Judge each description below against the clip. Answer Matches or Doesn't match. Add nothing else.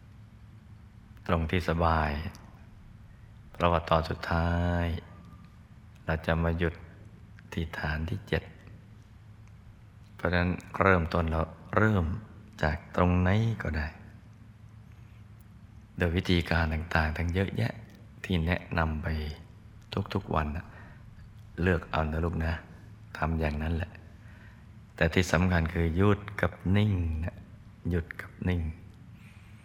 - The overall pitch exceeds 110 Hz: Doesn't match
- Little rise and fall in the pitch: Doesn't match